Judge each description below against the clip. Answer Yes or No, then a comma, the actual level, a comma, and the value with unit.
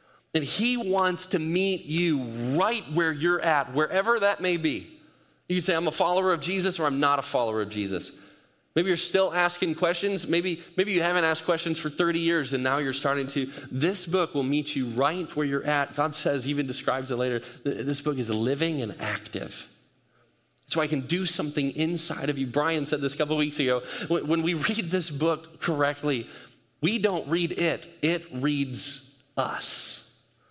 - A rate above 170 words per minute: Yes, average, 195 wpm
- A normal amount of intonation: Yes, average, 3.9 semitones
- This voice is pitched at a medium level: Yes, medium, 155 Hz